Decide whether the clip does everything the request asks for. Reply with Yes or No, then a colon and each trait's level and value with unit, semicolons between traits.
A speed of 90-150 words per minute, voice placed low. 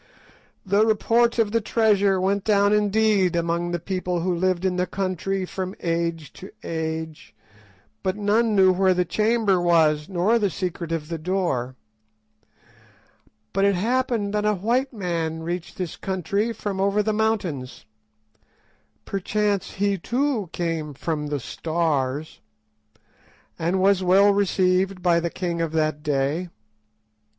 No: slow, 135 wpm; medium, 185 Hz